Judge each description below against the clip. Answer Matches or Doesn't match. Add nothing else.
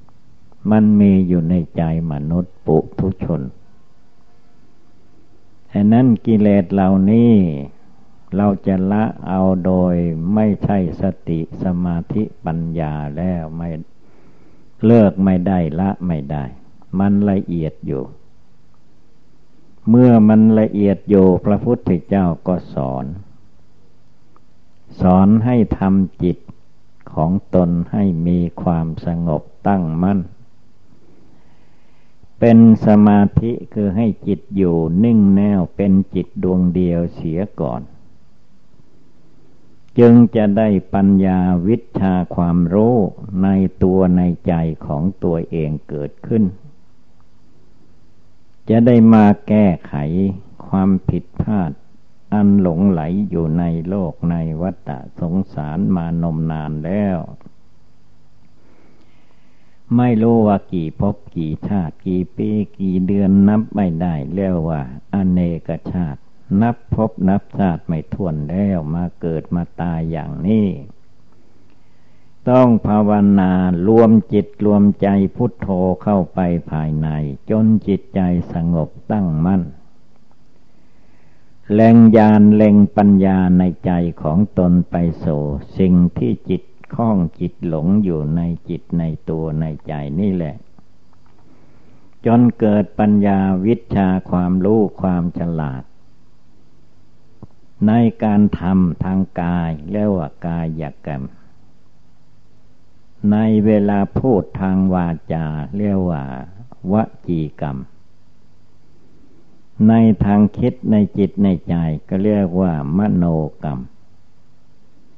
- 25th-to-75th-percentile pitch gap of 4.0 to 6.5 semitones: Doesn't match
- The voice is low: Matches